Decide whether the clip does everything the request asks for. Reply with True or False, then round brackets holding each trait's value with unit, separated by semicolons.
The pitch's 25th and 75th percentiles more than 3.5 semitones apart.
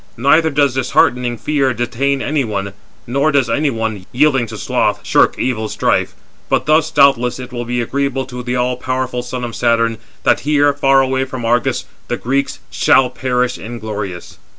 False (2.7 semitones)